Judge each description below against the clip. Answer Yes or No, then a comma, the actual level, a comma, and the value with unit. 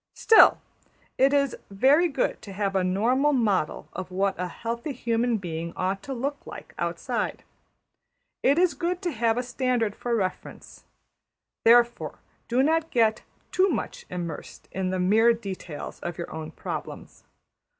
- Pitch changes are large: Yes, wide, 6.0 semitones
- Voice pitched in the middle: No, high, 230 Hz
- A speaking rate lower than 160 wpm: Yes, average, 150 wpm